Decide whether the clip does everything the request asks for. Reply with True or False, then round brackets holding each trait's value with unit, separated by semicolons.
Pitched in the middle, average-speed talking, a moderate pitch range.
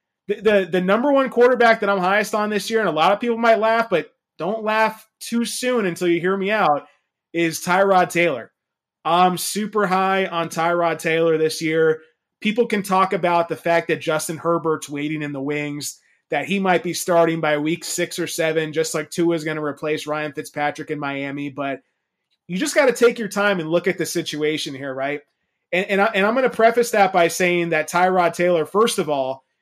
False (175 Hz; 215 wpm; 4.5 semitones)